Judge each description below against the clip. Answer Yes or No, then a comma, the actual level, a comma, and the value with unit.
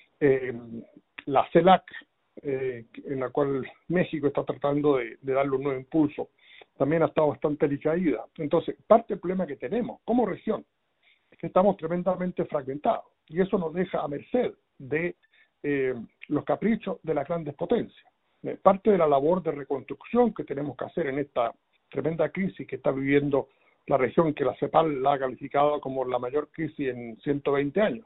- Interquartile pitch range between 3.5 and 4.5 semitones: Yes, average, 4.1 semitones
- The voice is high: No, medium, 150 Hz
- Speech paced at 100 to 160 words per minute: No, average, 175 wpm